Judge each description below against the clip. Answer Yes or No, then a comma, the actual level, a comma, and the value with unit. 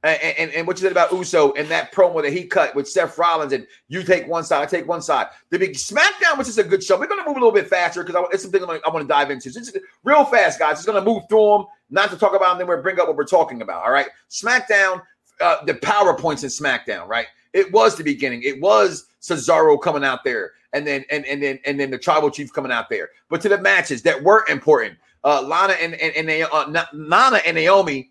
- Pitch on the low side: No, medium, 185 Hz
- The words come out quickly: Yes, fast, 270 wpm